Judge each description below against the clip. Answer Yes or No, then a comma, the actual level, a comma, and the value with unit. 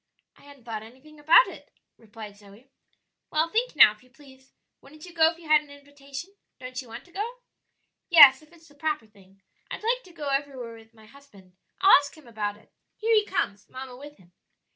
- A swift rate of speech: Yes, fast, 210 wpm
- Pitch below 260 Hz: No, very high, 280 Hz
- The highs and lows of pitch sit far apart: Yes, wide, 5.7 semitones